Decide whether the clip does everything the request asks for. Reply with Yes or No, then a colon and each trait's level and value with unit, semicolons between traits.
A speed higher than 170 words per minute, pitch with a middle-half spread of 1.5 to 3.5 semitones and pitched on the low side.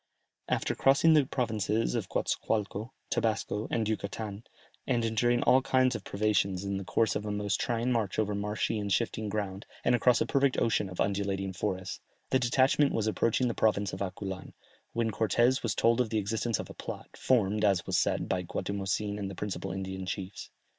Yes: average, 190 wpm; average, 3.0 semitones; low, 105 Hz